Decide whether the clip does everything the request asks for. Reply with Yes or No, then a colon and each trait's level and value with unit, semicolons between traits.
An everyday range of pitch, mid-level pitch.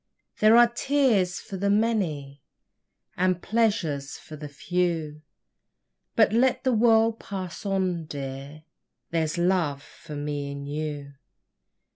No: wide, 6.6 semitones; medium, 175 Hz